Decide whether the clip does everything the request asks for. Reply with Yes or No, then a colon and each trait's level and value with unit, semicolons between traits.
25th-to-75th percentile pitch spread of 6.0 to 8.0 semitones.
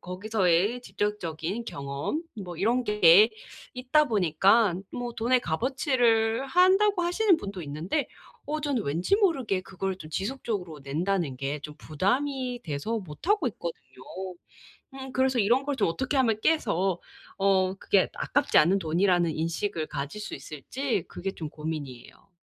Yes: wide, 7.4 semitones